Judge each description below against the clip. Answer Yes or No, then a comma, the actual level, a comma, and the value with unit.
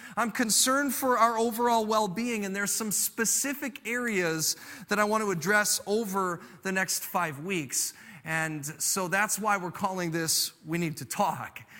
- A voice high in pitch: Yes, high, 205 Hz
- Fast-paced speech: No, average, 165 wpm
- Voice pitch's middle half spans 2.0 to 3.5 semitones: No, average, 4.5 semitones